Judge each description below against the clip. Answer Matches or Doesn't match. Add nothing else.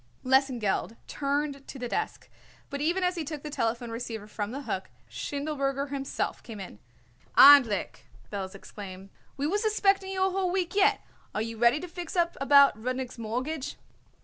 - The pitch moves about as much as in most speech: Doesn't match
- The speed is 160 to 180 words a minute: Matches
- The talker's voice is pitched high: Matches